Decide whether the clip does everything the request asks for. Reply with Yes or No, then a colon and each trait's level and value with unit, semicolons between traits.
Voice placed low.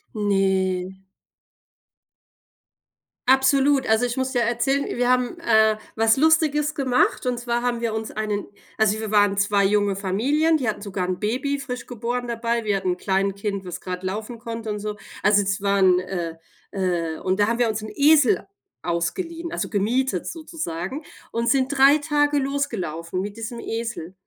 No: high, 220 Hz